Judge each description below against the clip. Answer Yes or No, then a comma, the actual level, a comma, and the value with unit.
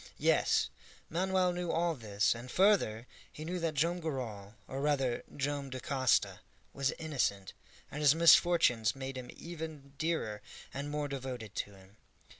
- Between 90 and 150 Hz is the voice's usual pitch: Yes, medium, 140 Hz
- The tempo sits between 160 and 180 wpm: No, average, 145 wpm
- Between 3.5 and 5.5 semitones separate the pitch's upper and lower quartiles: Yes, average, 5.1 semitones